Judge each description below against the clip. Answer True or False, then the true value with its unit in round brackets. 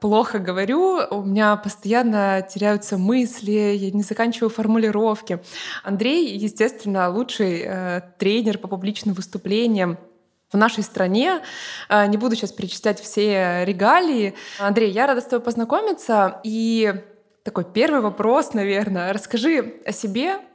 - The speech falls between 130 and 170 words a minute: False (120 wpm)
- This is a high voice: True (210 Hz)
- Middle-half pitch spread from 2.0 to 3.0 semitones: True (2.6 semitones)